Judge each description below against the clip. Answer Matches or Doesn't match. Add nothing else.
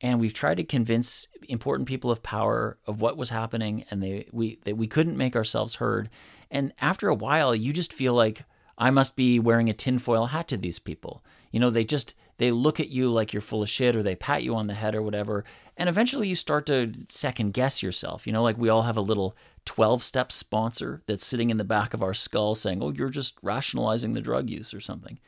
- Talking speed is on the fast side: Matches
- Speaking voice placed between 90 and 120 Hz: Matches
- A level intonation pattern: Doesn't match